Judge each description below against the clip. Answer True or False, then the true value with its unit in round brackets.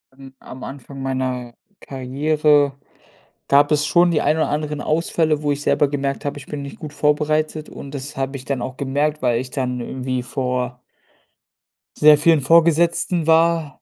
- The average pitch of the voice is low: False (145 Hz)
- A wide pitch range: False (2.5 semitones)